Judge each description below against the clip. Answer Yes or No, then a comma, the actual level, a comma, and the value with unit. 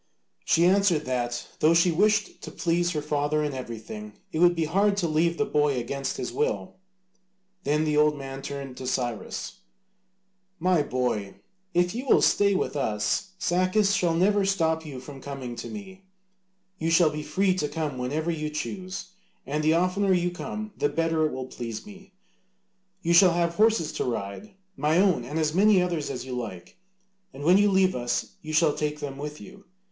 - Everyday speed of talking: Yes, average, 185 wpm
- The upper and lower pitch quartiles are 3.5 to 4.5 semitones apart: No, average, 4.9 semitones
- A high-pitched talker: No, medium, 160 Hz